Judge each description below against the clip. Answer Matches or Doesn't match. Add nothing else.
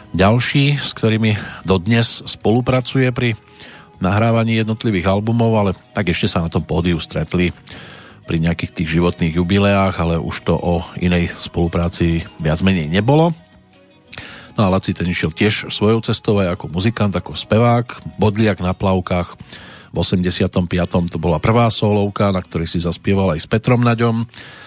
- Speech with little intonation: Doesn't match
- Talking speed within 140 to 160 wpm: Matches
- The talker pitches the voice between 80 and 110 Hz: Matches